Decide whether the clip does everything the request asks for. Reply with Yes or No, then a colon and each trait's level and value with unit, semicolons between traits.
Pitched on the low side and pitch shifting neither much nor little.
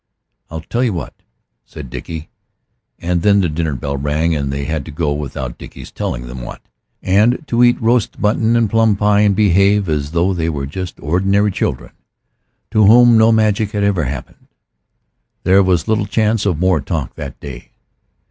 No: very low, 95 Hz; wide, 5.8 semitones